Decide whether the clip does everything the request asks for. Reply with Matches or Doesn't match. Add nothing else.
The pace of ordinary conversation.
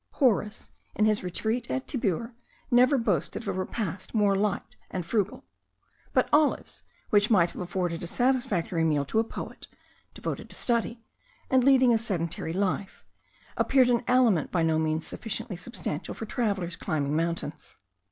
Matches